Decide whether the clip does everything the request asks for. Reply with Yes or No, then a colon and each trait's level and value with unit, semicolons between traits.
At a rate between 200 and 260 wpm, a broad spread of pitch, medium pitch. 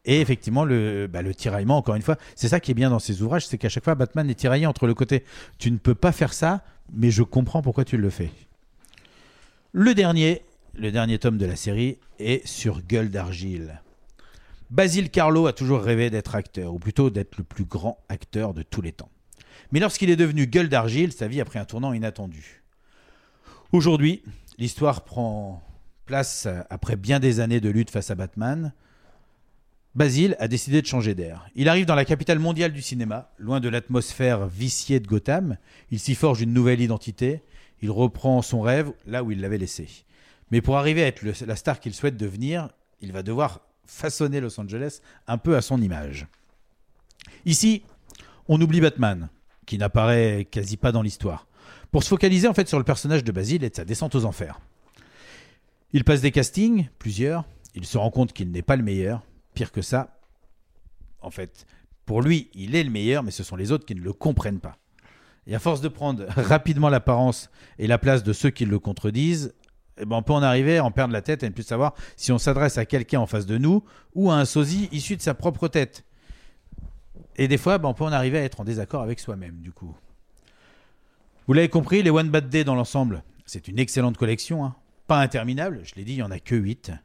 No: average, 210 wpm; wide, 5.8 semitones; low, 125 Hz